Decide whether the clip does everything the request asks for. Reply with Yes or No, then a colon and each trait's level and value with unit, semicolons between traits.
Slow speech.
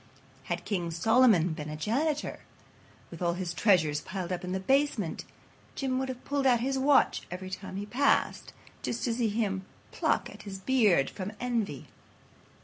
No: average, 170 wpm